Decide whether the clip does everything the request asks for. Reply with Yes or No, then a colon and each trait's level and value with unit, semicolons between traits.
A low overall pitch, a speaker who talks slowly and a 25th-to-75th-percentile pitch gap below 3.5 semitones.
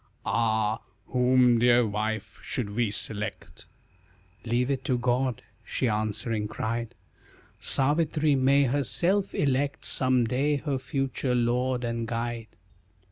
Yes: low, 125 Hz; slow, 115 wpm; average, 2.9 semitones